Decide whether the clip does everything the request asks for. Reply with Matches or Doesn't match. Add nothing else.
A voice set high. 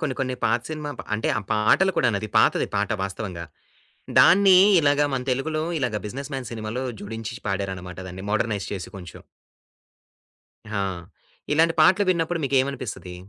Doesn't match